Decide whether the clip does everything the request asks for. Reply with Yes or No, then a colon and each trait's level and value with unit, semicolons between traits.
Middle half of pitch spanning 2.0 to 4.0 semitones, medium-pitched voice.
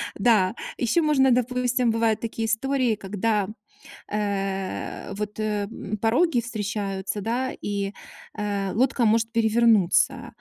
No: average, 2.8 semitones; high, 220 Hz